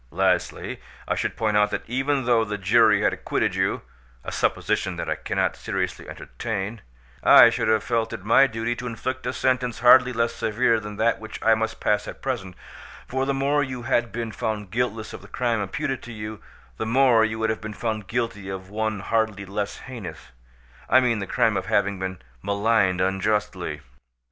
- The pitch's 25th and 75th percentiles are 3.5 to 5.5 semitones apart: No, average, 2.9 semitones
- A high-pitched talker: No, low, 110 Hz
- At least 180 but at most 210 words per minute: Yes, average, 185 wpm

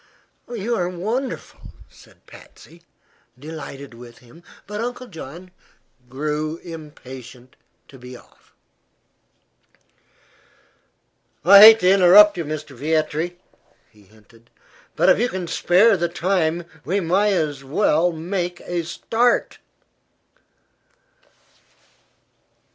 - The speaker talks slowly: Yes, slow, 105 wpm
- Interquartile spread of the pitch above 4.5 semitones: Yes, average, 5.1 semitones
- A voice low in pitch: No, medium, 170 Hz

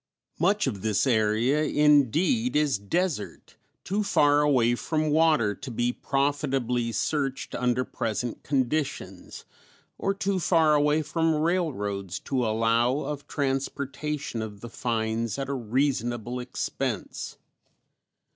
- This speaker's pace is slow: Yes, slow, 120 wpm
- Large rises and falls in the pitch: No, average, 4.5 semitones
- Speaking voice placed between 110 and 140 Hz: Yes, low, 135 Hz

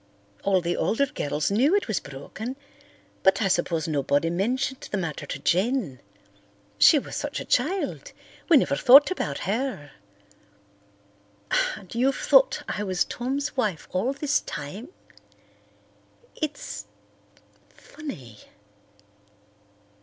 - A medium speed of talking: No, slow, 115 wpm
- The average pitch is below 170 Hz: No, high, 215 Hz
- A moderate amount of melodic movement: No, wide, 8.3 semitones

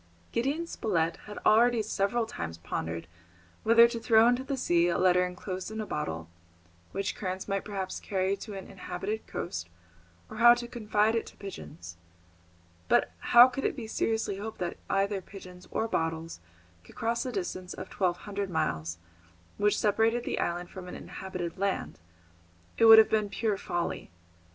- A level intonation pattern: No, average, 3.7 semitones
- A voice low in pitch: No, high, 200 Hz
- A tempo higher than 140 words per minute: Yes, average, 165 wpm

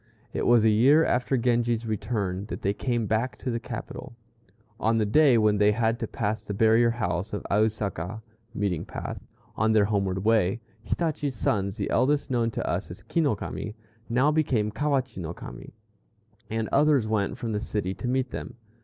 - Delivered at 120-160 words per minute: No, average, 185 wpm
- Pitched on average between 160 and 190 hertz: No, low, 110 Hz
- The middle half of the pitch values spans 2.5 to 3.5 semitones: Yes, average, 3.0 semitones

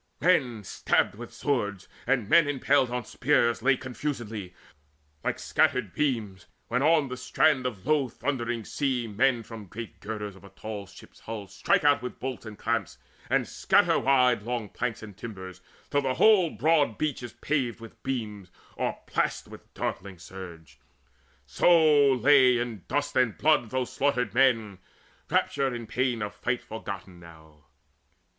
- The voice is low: Yes, low, 120 Hz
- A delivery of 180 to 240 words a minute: No, average, 160 wpm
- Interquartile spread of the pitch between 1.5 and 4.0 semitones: No, average, 4.4 semitones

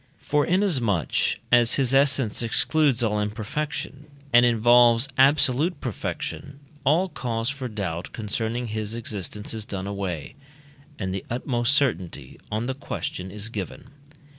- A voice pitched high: No, low, 120 Hz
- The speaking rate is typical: No, slow, 130 wpm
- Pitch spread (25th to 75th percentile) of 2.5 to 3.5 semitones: No, average, 4.8 semitones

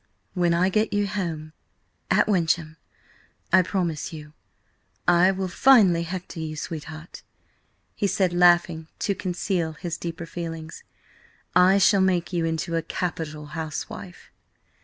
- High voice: No, medium, 175 Hz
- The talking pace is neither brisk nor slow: No, slow, 130 wpm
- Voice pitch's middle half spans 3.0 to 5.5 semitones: No, narrow, 2.6 semitones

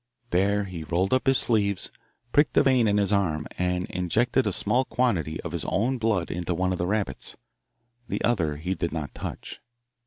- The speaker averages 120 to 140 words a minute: No, average, 190 wpm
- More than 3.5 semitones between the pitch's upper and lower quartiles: Yes, average, 4.5 semitones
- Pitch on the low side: Yes, very low, 95 Hz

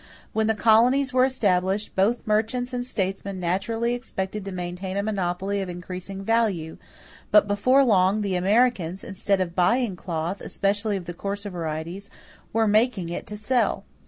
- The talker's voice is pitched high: Yes, high, 200 Hz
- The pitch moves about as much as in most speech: Yes, average, 3.5 semitones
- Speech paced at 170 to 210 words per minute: No, average, 160 wpm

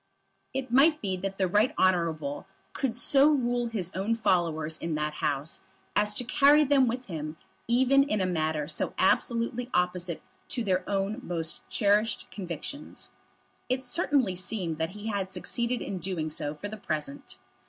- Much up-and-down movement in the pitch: Yes, wide, 6.4 semitones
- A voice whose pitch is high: Yes, high, 195 Hz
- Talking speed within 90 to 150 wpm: No, average, 165 wpm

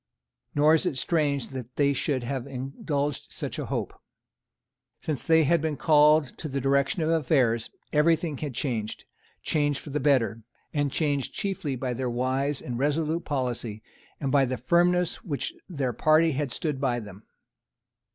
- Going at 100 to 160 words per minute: No, average, 170 wpm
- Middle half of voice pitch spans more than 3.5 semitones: No, average, 3.2 semitones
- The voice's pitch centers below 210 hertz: Yes, medium, 140 Hz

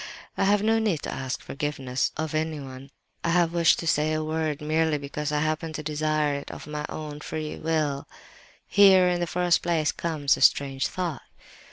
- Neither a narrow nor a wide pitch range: No, narrow, 2.2 semitones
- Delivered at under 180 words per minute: No, average, 185 wpm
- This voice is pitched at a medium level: Yes, medium, 155 Hz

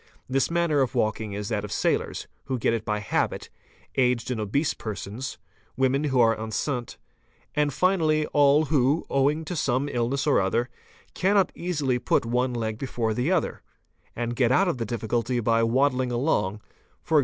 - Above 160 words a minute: Yes, average, 170 wpm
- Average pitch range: Yes, average, 4.0 semitones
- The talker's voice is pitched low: Yes, low, 130 Hz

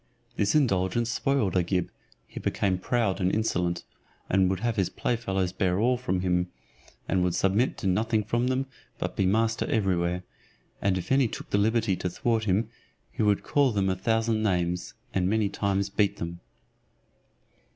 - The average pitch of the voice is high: No, low, 100 Hz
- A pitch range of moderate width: Yes, average, 3.5 semitones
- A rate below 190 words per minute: Yes, average, 170 wpm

